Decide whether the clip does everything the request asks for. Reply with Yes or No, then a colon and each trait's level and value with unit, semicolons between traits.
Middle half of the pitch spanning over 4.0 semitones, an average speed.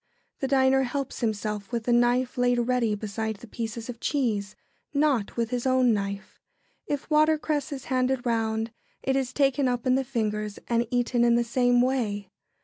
No: average, 3.0 semitones; average, 180 wpm